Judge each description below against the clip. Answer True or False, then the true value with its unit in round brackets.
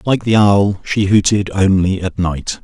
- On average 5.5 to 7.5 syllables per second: False (4.1 syllables/s)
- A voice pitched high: False (100 Hz)